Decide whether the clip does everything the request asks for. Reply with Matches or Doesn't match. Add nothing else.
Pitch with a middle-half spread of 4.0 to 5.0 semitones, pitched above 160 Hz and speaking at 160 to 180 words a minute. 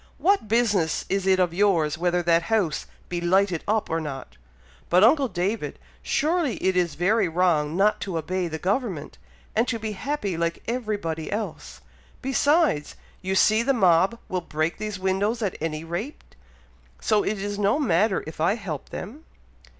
Matches